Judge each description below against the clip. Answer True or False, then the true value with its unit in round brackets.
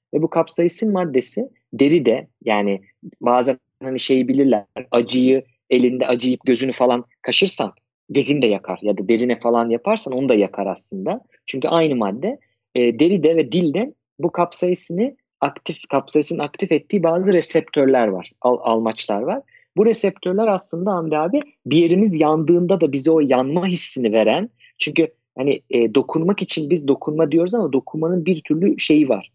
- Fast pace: True (155 wpm)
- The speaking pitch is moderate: True (150 Hz)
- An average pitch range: False (5.7 semitones)